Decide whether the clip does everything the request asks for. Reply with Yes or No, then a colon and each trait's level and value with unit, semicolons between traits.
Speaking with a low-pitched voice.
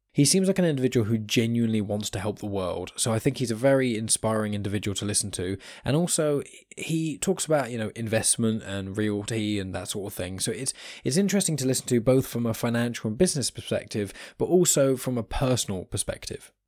Yes: low, 115 Hz